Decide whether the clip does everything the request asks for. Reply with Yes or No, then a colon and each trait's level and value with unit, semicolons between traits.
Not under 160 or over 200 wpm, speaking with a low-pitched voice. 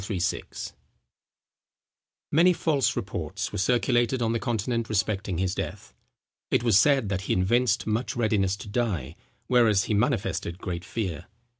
No: average, 140 wpm; low, 110 Hz